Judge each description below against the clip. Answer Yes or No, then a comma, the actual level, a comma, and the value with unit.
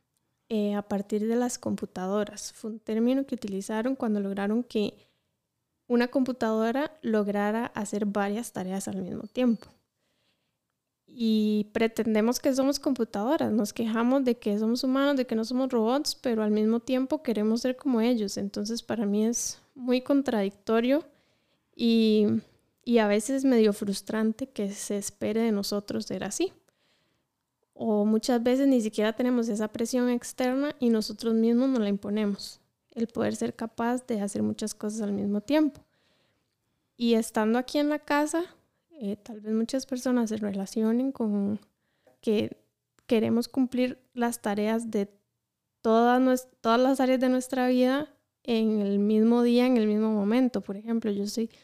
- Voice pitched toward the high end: Yes, high, 230 Hz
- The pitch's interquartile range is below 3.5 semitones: Yes, average, 3.0 semitones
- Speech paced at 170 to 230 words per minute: No, average, 150 wpm